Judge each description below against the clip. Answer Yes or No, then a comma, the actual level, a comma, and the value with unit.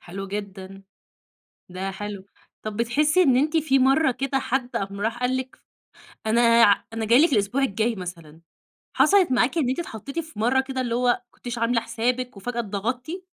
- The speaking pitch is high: Yes, high, 240 Hz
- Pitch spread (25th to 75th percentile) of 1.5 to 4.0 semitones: No, average, 4.4 semitones